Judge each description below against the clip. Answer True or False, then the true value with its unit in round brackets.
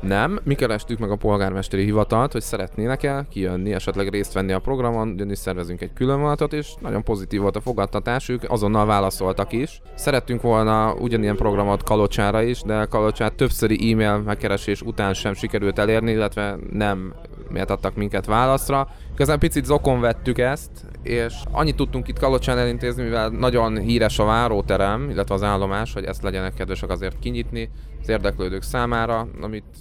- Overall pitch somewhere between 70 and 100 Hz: False (110 Hz)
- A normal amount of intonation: True (3.4 semitones)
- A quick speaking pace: True (160 wpm)